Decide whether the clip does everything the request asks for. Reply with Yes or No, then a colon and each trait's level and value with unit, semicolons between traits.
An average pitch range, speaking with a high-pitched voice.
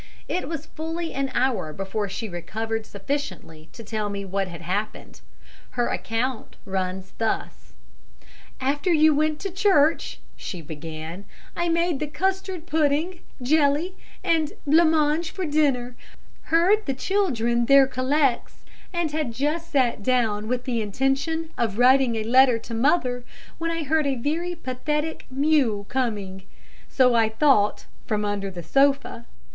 No: wide, 6.2 semitones; very high, 265 Hz